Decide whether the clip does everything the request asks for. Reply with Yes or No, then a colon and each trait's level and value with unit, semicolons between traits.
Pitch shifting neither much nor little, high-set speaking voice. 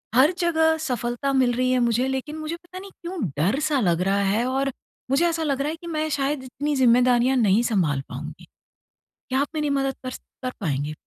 Yes: average, 4.3 semitones; very high, 265 Hz